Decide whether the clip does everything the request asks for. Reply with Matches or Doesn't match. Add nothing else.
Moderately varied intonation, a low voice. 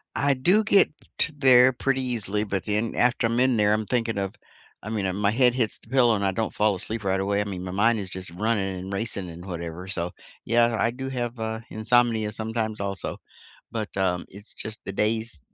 Matches